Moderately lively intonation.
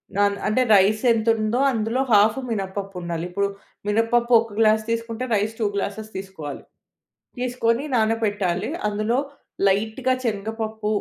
No: narrow, 2.2 semitones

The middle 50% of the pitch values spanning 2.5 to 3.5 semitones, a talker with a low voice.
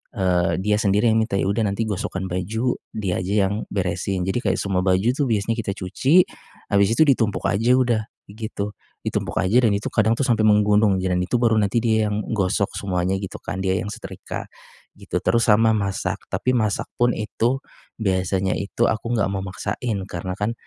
Yes: average, 2.8 semitones; low, 105 Hz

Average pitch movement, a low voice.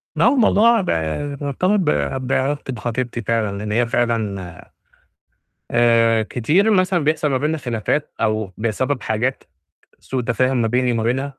Yes: average, 4.2 semitones; low, 125 Hz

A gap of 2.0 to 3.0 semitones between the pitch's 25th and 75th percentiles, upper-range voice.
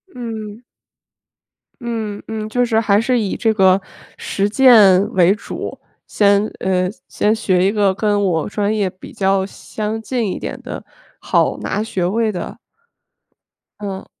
Yes: narrow, 2.4 semitones; high, 205 Hz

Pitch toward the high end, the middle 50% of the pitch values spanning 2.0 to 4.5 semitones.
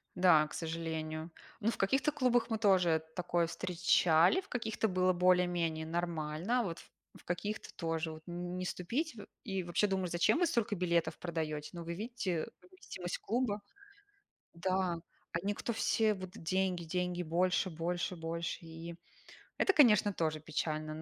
No: medium, 180 Hz; average, 3.6 semitones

